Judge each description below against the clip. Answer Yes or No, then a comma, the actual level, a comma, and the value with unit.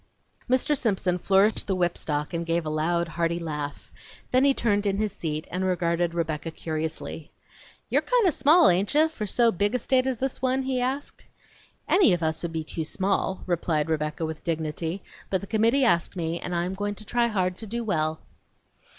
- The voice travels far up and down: Yes, wide, 6.0 semitones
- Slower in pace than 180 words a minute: No, average, 200 wpm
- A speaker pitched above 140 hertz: Yes, medium, 185 Hz